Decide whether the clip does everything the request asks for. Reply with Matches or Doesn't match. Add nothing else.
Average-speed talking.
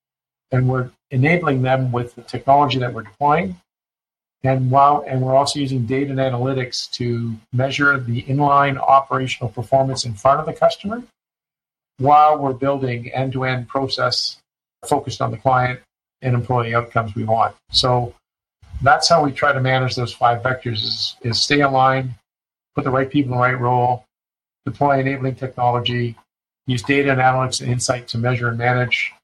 Matches